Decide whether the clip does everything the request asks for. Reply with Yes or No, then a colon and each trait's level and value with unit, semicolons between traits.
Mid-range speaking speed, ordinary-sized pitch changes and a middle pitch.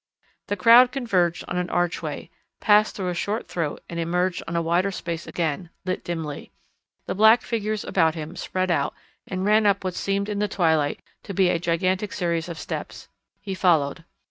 Yes: average, 185 wpm; average, 3.2 semitones; medium, 180 Hz